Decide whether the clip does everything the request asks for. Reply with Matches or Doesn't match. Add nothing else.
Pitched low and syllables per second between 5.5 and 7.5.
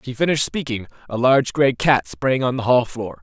Matches